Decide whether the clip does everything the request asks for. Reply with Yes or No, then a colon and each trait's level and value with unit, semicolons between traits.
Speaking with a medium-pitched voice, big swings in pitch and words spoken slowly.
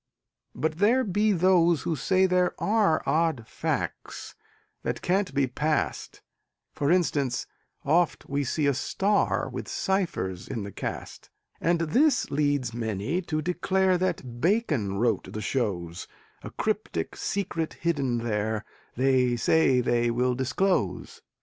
Yes: medium, 150 Hz; wide, 7.2 semitones; slow, 130 wpm